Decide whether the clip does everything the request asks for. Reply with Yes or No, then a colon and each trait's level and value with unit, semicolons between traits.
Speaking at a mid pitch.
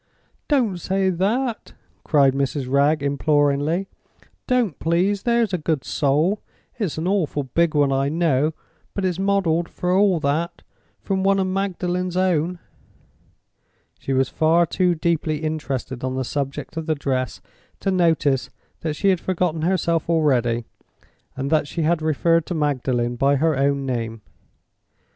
Yes: medium, 160 Hz